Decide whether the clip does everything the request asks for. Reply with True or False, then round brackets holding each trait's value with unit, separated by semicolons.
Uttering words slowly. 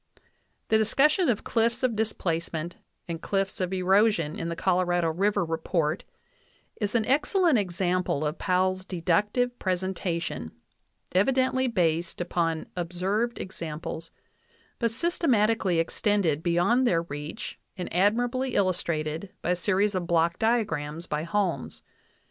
True (125 wpm)